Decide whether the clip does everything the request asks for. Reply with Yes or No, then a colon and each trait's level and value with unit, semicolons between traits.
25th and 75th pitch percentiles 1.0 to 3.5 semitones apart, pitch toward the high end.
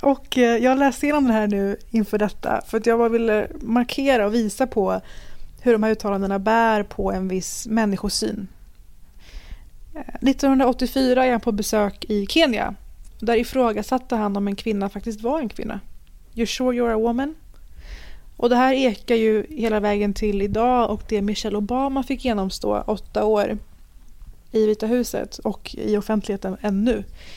Yes: average, 3.1 semitones; high, 220 Hz